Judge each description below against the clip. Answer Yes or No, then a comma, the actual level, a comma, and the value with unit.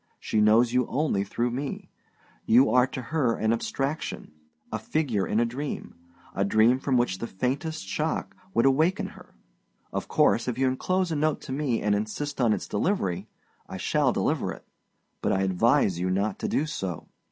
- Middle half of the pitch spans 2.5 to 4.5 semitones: No, average, 5.1 semitones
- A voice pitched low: Yes, low, 125 Hz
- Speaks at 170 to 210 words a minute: Yes, average, 185 wpm